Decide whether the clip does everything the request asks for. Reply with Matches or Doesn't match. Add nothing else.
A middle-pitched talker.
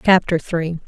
Matches